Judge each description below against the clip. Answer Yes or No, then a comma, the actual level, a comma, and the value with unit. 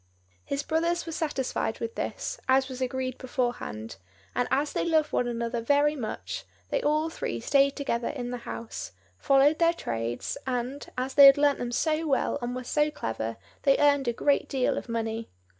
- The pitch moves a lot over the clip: No, average, 3.7 semitones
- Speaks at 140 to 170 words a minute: No, average, 185 wpm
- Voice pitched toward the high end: Yes, very high, 260 Hz